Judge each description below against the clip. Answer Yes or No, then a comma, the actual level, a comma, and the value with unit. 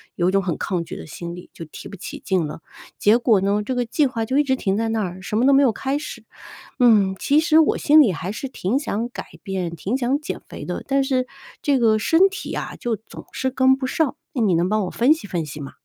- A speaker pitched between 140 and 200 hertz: No, high, 225 Hz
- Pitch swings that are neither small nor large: No, wide, 5.9 semitones